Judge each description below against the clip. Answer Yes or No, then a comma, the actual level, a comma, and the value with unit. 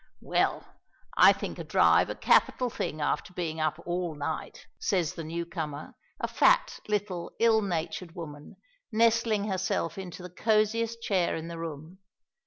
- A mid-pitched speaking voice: Yes, medium, 175 Hz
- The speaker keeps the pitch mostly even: No, average, 4.6 semitones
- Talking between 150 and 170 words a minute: Yes, average, 155 wpm